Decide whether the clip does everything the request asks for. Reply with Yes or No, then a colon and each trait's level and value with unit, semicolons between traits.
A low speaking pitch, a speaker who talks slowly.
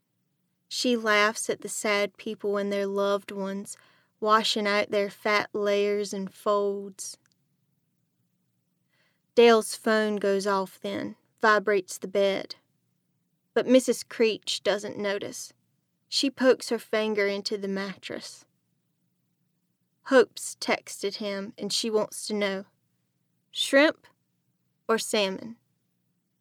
No: high, 205 Hz; slow, 110 wpm